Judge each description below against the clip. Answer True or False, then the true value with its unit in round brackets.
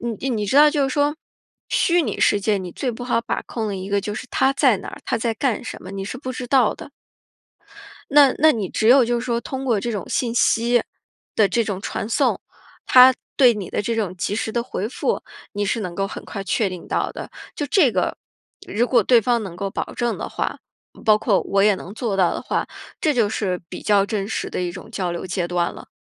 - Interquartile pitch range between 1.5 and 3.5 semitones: False (4.0 semitones)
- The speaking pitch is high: True (220 Hz)